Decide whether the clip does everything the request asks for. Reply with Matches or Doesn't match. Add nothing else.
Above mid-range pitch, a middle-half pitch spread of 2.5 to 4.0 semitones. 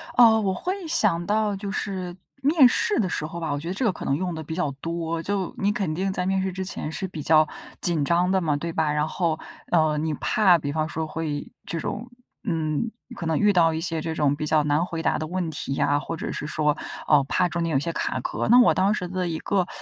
Doesn't match